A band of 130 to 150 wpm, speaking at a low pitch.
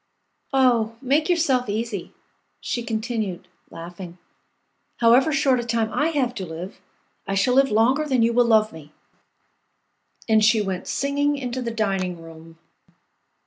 No: average, 145 wpm; high, 230 Hz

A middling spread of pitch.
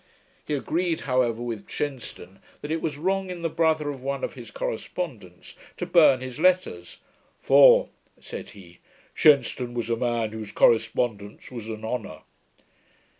No: wide, 5.8 semitones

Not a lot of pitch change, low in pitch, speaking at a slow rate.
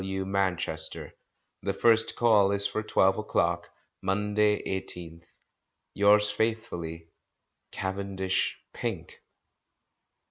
Yes: narrow, 1.8 semitones; low, 100 Hz; slow, 100 wpm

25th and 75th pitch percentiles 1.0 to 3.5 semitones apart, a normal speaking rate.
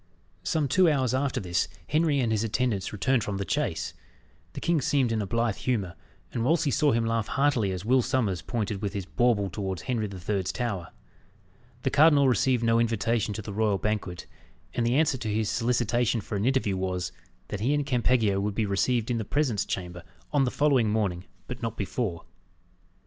No: average, 4.2 semitones; average, 195 wpm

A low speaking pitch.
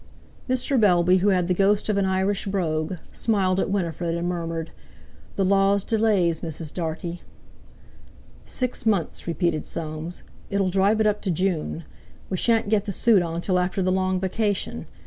No: medium, 185 Hz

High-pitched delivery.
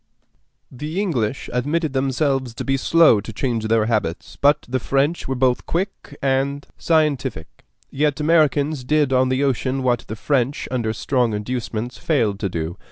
No: low, 130 Hz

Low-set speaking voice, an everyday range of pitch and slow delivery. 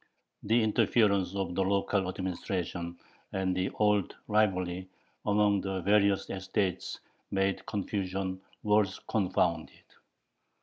No: very low, 95 Hz; narrow, 1.8 semitones; slow, 100 wpm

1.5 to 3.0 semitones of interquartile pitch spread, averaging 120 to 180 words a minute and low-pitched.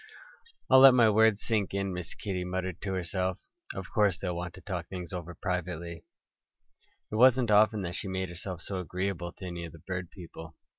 No: narrow, 2.5 semitones; average, 195 wpm; very low, 95 Hz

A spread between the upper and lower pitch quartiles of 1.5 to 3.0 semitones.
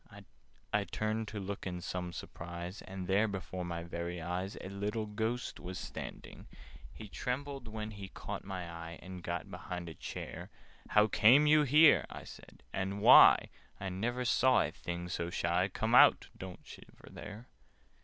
No: average, 3.8 semitones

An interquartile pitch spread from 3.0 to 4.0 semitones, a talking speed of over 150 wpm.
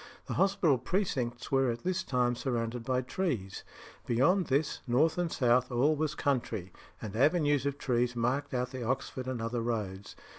Yes: average, 3.6 semitones; average, 170 wpm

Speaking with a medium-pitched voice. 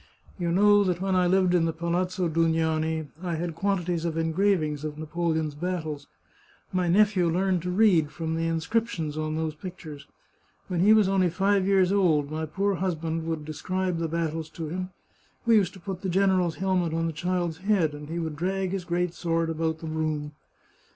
Yes: medium, 170 Hz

